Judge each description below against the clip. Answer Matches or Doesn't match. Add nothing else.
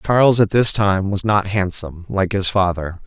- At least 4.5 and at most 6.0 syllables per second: Matches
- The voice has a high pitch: Doesn't match